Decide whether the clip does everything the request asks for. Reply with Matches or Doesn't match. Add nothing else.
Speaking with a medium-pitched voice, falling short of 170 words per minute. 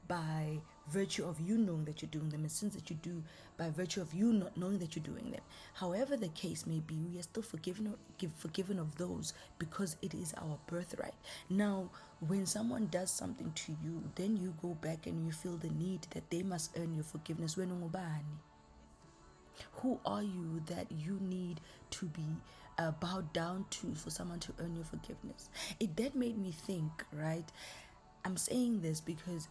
Doesn't match